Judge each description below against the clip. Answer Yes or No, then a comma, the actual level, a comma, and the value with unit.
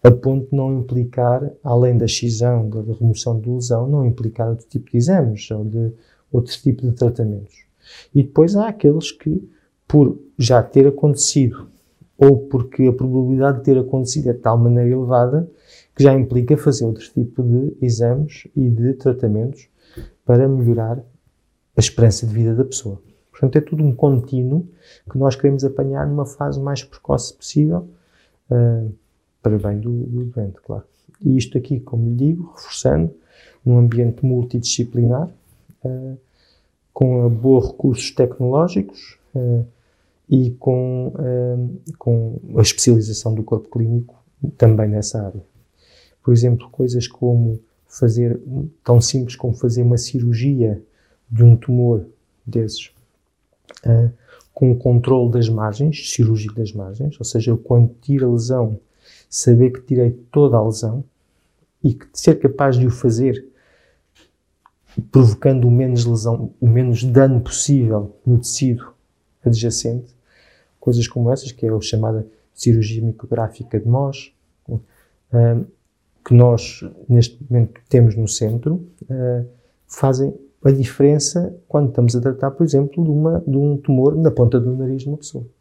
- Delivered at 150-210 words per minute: No, average, 140 wpm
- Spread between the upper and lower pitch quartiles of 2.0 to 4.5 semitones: Yes, average, 2.7 semitones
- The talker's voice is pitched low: Yes, low, 125 Hz